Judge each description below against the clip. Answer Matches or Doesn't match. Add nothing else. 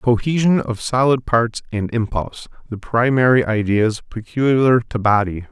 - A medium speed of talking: Doesn't match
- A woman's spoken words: Doesn't match